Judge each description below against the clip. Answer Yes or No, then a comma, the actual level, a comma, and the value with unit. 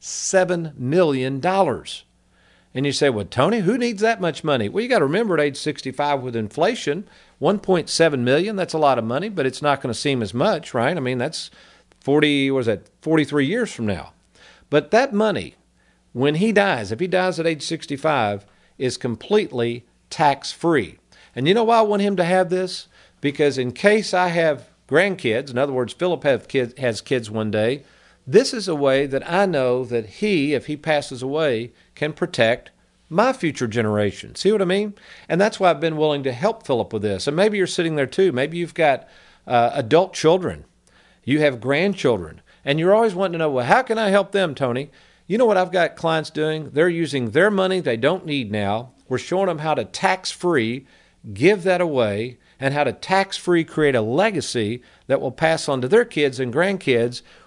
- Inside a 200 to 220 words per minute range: Yes, fast, 205 wpm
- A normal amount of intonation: No, wide, 6.2 semitones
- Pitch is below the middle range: No, medium, 150 Hz